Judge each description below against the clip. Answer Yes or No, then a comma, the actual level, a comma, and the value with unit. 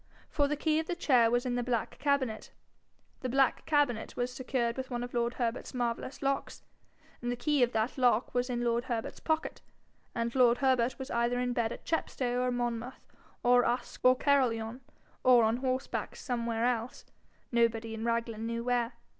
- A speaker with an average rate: Yes, average, 180 wpm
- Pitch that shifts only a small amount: Yes, narrow, 1.7 semitones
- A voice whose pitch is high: Yes, high, 245 Hz